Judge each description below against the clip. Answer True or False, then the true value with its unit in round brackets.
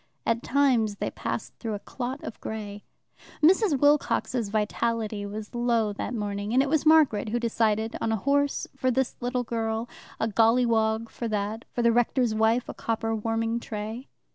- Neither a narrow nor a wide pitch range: False (2.3 semitones)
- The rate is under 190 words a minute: True (170 wpm)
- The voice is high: True (230 Hz)